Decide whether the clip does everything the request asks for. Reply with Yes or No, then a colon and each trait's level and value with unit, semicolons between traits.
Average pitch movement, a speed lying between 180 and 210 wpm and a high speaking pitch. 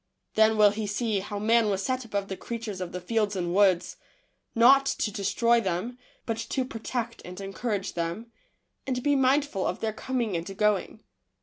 Yes: average, 3.3 semitones; average, 185 wpm; high, 215 Hz